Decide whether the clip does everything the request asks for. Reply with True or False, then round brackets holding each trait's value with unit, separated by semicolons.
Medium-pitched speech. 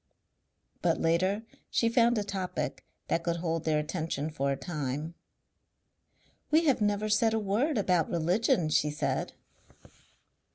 True (175 Hz)